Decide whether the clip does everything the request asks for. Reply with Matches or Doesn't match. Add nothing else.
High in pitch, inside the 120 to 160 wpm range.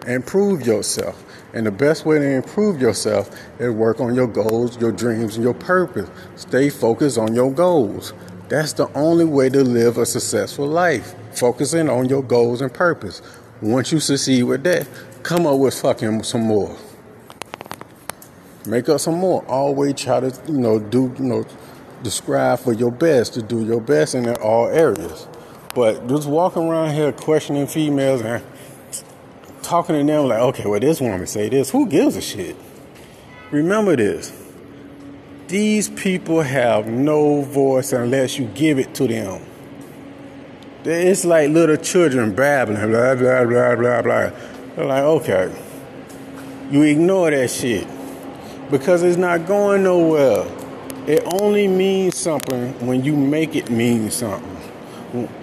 Doesn't match